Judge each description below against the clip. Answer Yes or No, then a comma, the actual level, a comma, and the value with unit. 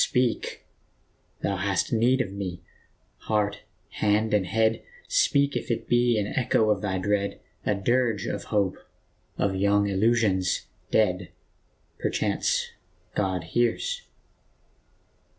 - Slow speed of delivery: Yes, slow, 115 wpm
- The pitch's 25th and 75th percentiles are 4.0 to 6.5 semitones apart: No, average, 3.2 semitones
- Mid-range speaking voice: No, low, 105 Hz